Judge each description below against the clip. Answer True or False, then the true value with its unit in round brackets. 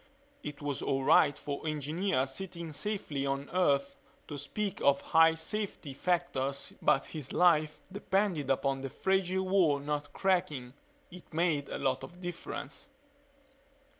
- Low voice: False (155 Hz)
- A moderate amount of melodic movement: True (4.5 semitones)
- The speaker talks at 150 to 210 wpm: False (135 wpm)